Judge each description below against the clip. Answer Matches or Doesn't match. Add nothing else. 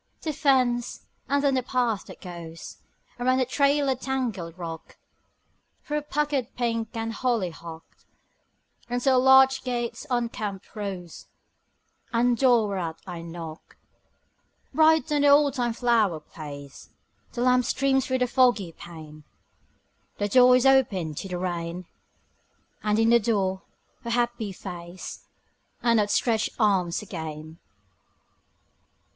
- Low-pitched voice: Doesn't match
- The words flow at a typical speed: Doesn't match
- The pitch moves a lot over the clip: Matches